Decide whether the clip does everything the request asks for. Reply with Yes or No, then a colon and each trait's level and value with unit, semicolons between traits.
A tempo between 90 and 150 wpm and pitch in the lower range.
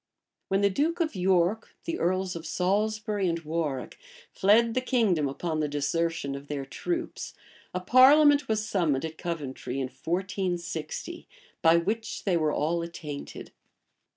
No: average, 145 wpm; medium, 180 Hz